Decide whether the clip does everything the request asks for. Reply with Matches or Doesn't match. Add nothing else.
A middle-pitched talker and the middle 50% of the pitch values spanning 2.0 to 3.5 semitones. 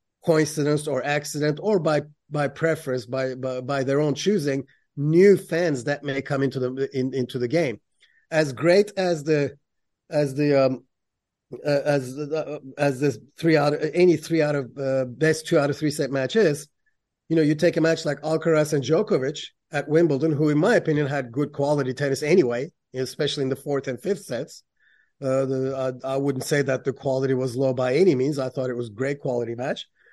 Matches